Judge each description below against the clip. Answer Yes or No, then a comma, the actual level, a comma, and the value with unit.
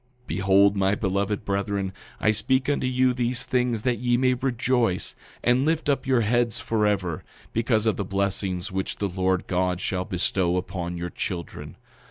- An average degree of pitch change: Yes, average, 4.5 semitones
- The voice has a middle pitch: No, low, 105 Hz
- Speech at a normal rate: Yes, average, 170 wpm